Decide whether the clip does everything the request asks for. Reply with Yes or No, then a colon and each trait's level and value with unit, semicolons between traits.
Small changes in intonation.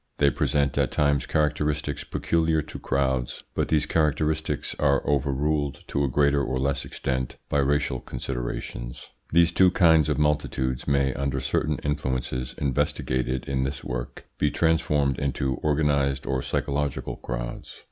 Yes: narrow, 2.3 semitones